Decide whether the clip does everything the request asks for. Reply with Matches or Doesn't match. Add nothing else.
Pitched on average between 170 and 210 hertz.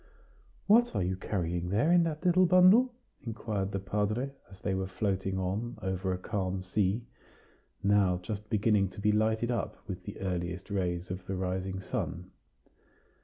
Doesn't match